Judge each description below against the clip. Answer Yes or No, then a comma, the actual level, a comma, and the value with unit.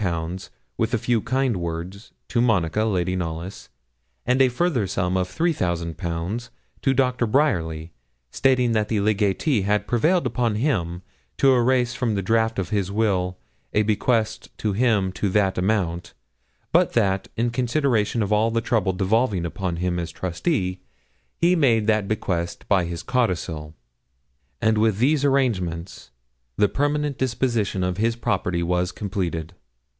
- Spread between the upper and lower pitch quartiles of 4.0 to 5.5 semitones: Yes, average, 5.0 semitones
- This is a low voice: Yes, low, 105 Hz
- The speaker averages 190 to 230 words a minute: No, average, 145 wpm